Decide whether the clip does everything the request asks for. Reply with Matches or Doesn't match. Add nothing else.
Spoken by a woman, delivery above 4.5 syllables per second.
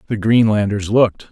Doesn't match